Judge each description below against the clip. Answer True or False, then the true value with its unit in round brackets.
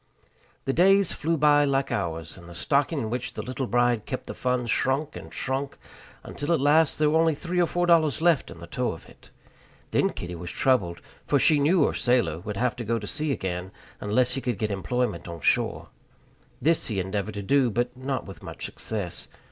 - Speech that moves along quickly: True (210 wpm)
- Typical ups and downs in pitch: False (6.4 semitones)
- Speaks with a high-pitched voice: False (125 Hz)